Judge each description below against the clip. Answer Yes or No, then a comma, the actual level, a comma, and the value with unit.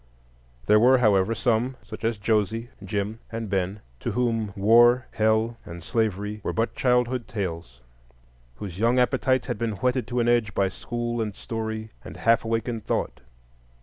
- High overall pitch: No, low, 110 Hz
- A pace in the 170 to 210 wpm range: No, average, 150 wpm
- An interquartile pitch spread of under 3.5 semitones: Yes, narrow, 2.5 semitones